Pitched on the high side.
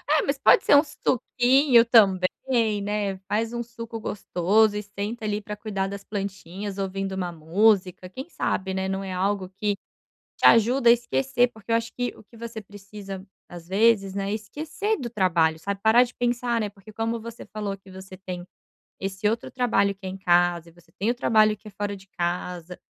Yes: high, 205 Hz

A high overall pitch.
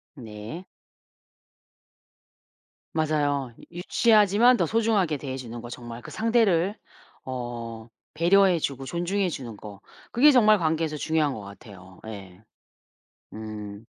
No: medium, 145 Hz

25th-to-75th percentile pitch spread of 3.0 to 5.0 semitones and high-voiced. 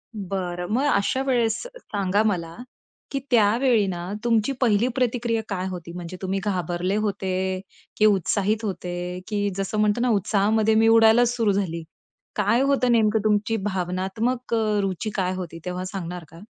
Yes: average, 3.4 semitones; high, 205 Hz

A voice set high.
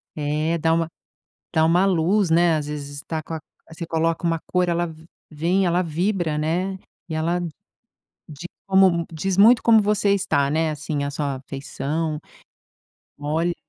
No: medium, 165 Hz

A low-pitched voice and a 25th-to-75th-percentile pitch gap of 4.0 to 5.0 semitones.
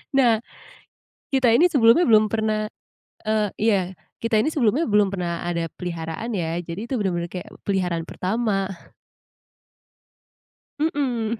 No: high, 215 Hz; average, 4.4 semitones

